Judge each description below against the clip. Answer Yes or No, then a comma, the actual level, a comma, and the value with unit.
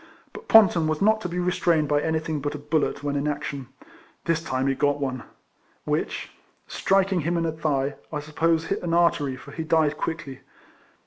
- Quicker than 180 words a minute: Yes, average, 190 wpm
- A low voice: No, medium, 155 Hz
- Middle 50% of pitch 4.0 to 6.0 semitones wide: No, average, 2.7 semitones